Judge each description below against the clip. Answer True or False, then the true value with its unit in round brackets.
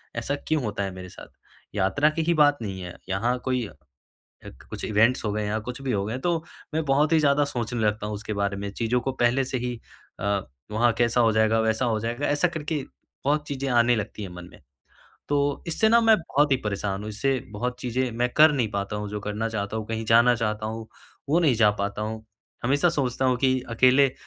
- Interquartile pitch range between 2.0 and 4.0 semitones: False (4.4 semitones)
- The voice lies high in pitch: False (120 Hz)